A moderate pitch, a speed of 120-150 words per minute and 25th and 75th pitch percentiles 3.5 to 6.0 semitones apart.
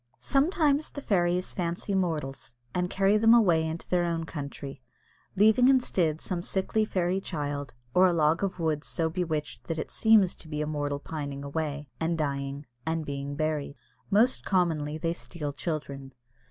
No: medium, 165 Hz; average, 165 wpm; average, 4.1 semitones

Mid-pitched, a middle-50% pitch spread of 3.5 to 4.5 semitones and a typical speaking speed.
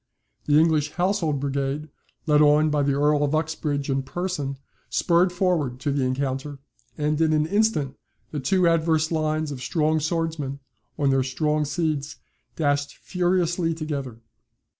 No: medium, 150 Hz; narrow, 2.5 semitones; average, 145 wpm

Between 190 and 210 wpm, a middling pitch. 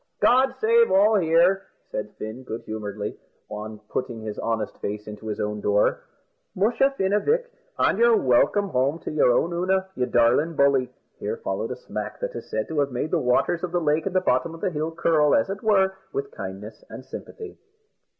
Yes: average, 200 wpm; medium, 150 Hz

